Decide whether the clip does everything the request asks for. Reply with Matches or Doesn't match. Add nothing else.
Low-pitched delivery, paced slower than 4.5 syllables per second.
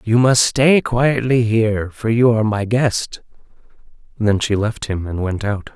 Matches